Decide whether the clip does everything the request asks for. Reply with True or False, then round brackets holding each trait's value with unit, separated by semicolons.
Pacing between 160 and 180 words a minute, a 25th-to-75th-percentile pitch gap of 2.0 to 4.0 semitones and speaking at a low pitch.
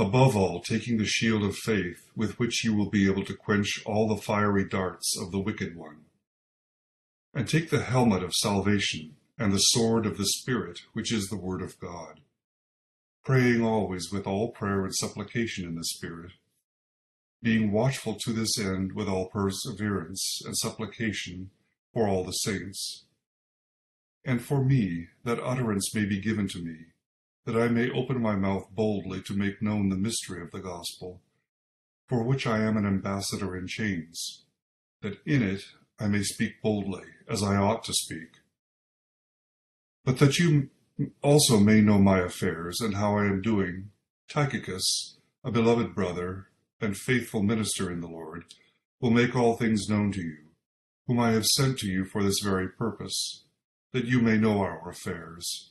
True (170 wpm; 3.2 semitones; 105 Hz)